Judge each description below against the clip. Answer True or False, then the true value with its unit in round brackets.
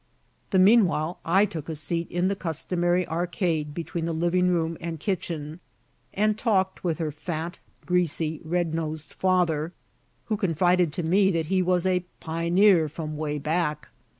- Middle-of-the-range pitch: True (170 Hz)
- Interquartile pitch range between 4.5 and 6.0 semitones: False (2.4 semitones)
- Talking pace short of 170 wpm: True (155 wpm)